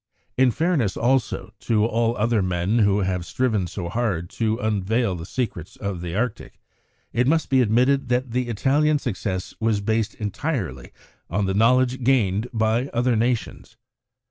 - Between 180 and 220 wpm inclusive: No, average, 155 wpm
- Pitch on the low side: Yes, low, 115 Hz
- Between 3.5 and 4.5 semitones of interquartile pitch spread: Yes, average, 4.0 semitones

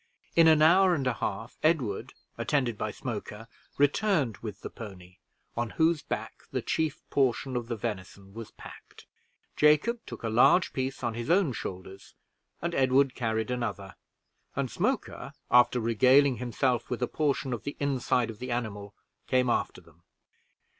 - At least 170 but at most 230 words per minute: No, average, 160 wpm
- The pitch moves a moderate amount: Yes, average, 4.2 semitones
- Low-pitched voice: Yes, low, 125 Hz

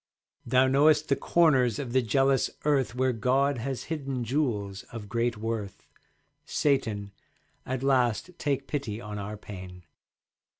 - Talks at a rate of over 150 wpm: No, slow, 135 wpm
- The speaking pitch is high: No, low, 125 Hz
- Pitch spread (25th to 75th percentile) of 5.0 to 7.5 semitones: No, average, 4.3 semitones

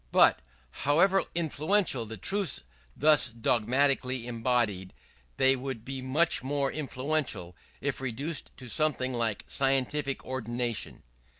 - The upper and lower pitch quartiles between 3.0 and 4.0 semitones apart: Yes, average, 3.7 semitones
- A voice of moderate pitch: No, low, 130 Hz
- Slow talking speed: Yes, slow, 110 wpm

